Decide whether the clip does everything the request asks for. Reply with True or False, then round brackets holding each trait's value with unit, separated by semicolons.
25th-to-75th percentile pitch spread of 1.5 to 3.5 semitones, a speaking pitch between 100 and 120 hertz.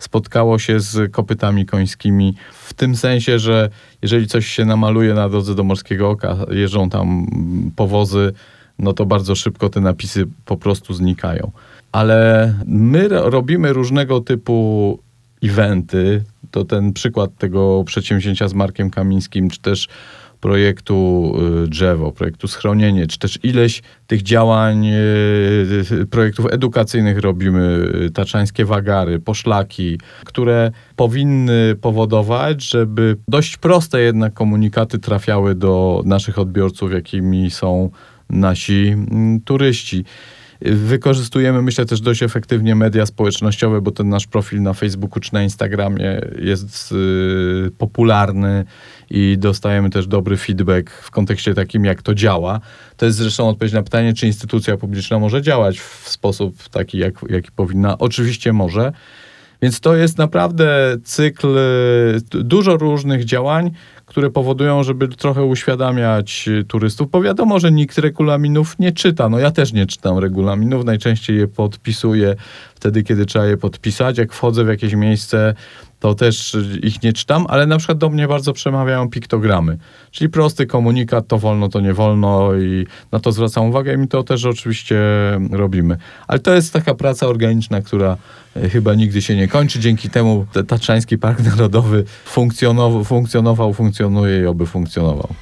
True (3.2 semitones; 110 Hz)